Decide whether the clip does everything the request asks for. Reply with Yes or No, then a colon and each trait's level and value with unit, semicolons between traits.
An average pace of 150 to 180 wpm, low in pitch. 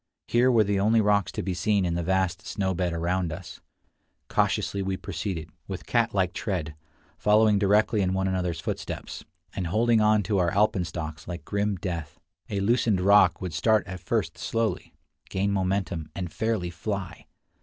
Yes: average, 170 wpm; very low, 95 Hz